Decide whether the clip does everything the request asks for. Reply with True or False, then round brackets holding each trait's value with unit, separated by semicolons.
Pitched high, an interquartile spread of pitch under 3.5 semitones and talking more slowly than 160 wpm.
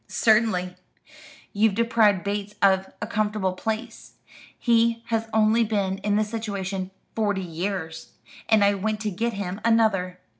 True (210 Hz; 2.6 semitones; 140 wpm)